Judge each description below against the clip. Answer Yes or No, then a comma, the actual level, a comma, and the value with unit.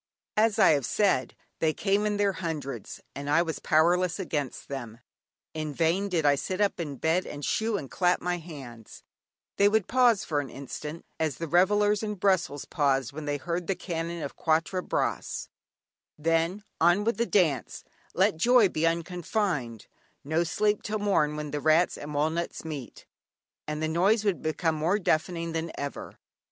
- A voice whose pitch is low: No, medium, 165 Hz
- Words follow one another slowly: No, average, 170 wpm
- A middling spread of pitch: Yes, average, 4.5 semitones